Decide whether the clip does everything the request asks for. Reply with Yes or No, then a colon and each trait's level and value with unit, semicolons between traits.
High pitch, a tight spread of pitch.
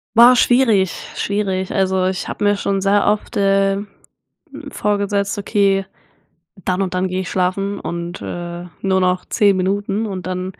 Yes: high, 195 Hz; narrow, 1.6 semitones